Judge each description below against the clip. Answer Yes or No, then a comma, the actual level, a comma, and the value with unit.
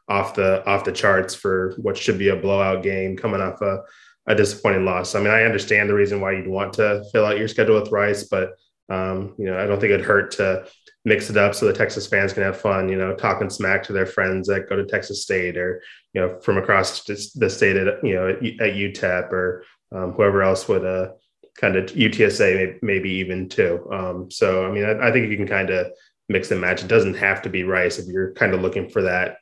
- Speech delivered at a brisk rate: Yes, fast, 240 wpm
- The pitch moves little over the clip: Yes, narrow, 1.5 semitones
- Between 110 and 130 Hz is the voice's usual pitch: No, very low, 95 Hz